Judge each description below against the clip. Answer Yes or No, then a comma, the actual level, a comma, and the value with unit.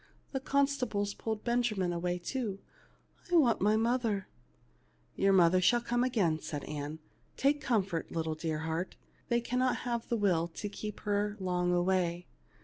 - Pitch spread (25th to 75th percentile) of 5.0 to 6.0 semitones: Yes, average, 5.3 semitones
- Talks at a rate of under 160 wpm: No, average, 165 wpm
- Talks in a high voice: Yes, high, 205 Hz